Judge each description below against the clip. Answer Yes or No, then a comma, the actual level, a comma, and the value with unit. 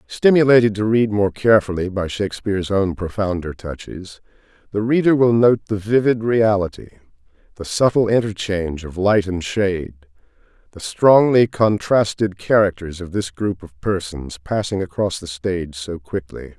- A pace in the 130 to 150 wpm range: Yes, average, 140 wpm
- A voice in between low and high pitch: No, low, 100 Hz